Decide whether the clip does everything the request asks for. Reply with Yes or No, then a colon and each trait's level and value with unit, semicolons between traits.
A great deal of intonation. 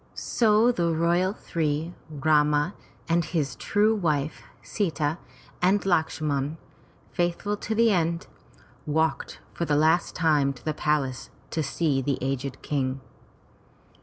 No: average, 3.1 semitones